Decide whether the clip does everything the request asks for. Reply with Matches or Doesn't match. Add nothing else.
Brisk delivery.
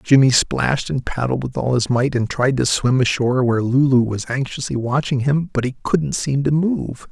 Matches